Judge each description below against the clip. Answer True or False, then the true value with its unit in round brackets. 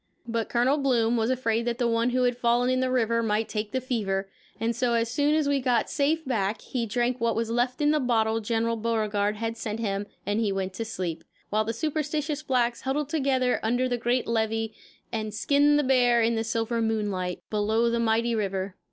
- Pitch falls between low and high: False (230 Hz)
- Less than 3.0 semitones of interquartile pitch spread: True (2.5 semitones)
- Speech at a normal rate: False (210 wpm)